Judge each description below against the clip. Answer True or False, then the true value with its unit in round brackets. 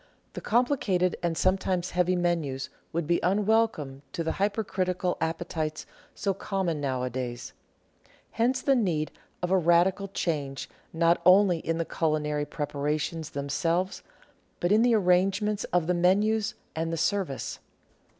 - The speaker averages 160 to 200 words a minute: False (135 wpm)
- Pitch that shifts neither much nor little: True (4.0 semitones)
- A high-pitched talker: False (175 Hz)